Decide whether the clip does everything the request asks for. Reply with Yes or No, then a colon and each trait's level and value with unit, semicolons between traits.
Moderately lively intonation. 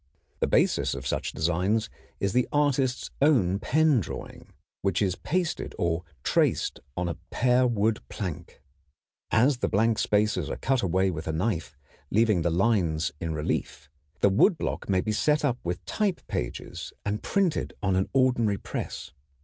No: wide, 6.3 semitones